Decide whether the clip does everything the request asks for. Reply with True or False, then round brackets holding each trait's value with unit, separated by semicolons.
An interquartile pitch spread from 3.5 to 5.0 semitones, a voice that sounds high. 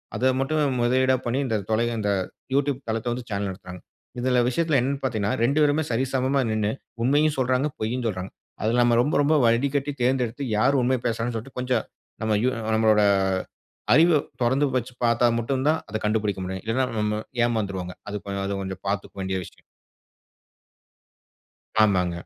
False (3.8 semitones; 120 Hz)